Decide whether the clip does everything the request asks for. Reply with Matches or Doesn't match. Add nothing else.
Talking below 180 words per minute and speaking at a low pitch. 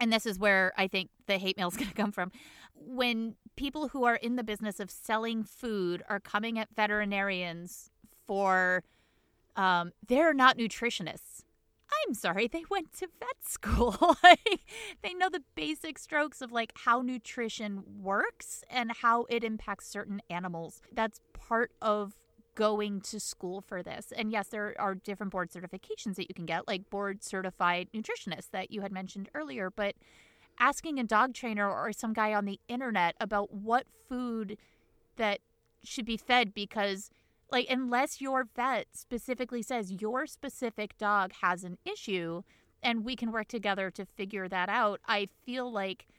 Doesn't match